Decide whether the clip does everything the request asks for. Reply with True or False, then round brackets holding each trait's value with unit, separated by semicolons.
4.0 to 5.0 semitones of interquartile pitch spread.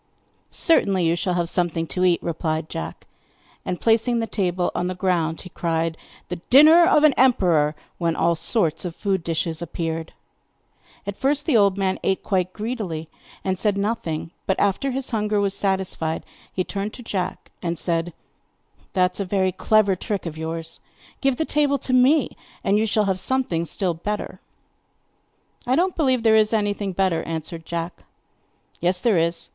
True (4.5 semitones)